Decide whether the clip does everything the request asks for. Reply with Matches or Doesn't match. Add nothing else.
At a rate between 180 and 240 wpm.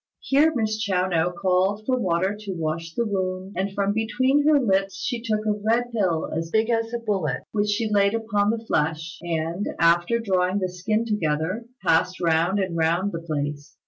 Matches